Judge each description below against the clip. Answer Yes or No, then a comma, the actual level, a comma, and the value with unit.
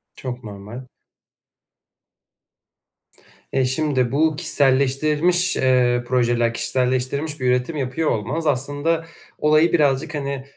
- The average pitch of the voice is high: No, low, 135 Hz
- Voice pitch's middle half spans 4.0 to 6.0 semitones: No, average, 3.3 semitones